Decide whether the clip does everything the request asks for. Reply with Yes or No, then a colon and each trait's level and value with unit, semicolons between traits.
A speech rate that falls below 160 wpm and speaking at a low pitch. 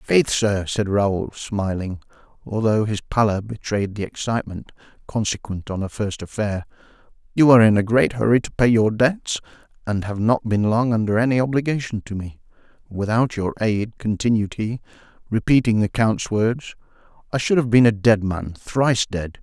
No: average, 165 wpm; low, 110 Hz